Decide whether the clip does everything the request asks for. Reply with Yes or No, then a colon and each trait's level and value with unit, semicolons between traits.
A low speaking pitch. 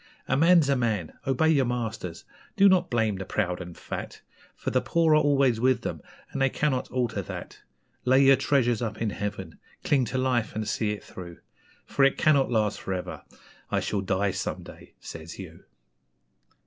Yes: low, 120 Hz